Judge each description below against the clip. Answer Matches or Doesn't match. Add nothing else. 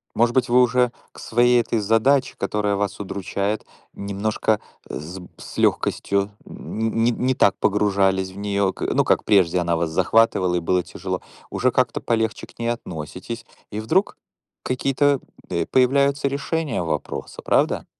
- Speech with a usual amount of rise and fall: Matches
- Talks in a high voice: Doesn't match